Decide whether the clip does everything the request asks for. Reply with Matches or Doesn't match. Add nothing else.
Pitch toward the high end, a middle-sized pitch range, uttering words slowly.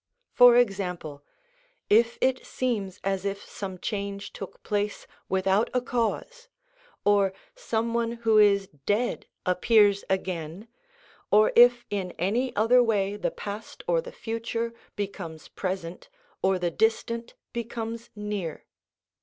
Matches